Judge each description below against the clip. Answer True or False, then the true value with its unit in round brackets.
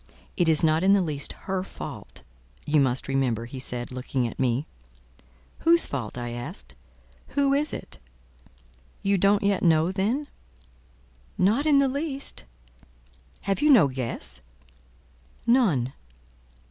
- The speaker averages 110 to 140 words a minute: True (135 wpm)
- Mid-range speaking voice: True (170 Hz)